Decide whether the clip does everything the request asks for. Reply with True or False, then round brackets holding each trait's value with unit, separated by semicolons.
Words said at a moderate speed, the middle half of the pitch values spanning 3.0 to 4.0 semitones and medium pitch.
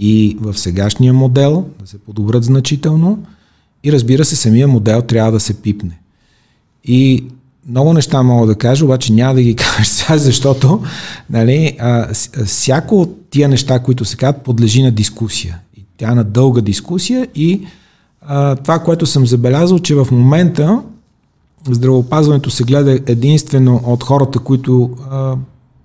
False (145 wpm; 3.7 semitones; 130 Hz)